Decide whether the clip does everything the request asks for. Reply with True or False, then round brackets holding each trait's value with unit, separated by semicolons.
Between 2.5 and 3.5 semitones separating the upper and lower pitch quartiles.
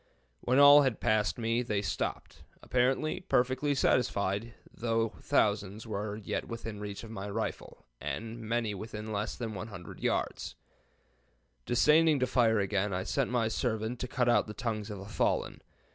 True (3.0 semitones)